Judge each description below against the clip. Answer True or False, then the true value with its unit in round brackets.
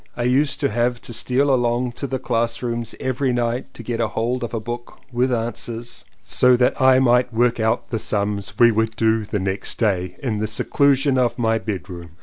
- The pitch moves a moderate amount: False (2.1 semitones)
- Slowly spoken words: False (200 wpm)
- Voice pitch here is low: True (120 Hz)